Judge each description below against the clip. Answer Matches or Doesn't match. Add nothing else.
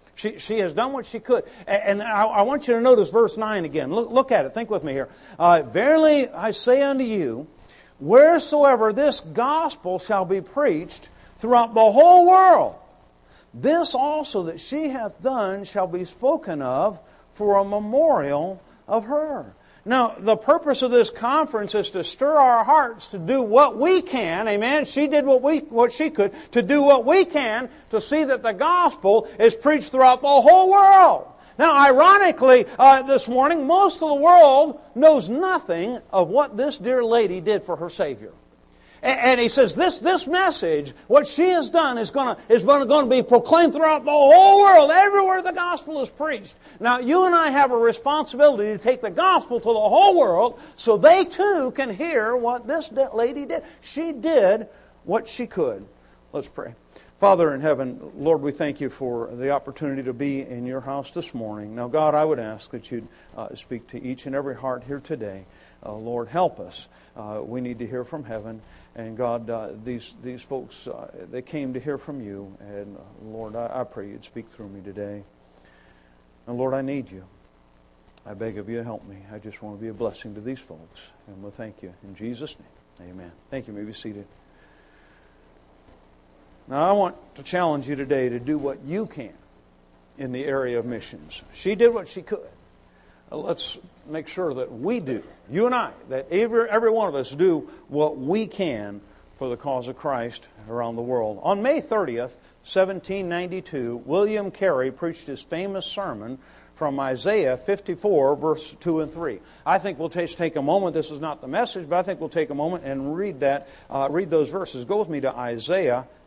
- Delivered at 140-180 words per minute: Doesn't match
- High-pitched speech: Matches